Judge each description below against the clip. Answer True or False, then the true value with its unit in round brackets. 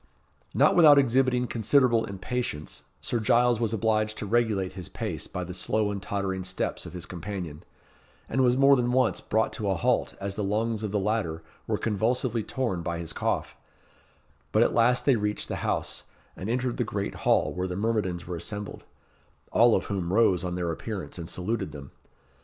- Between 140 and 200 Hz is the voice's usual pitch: False (105 Hz)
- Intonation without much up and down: False (4.3 semitones)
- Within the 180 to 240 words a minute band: True (185 wpm)